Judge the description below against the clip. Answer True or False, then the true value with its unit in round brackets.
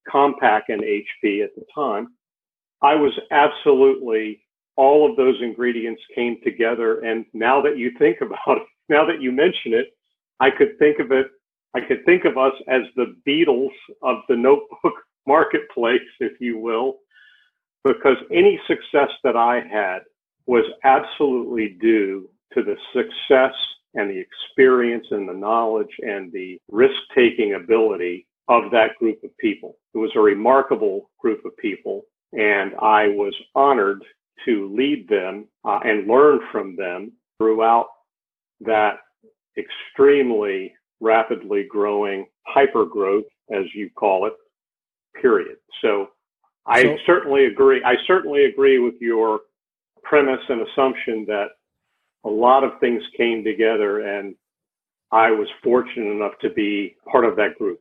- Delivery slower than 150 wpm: True (140 wpm)